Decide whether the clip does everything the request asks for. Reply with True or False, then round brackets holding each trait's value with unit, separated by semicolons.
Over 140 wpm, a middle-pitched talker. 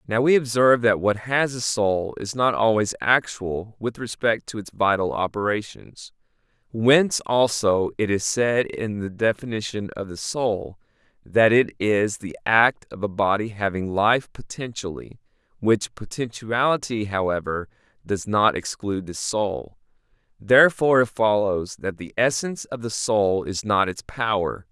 False (150 wpm; 110 Hz)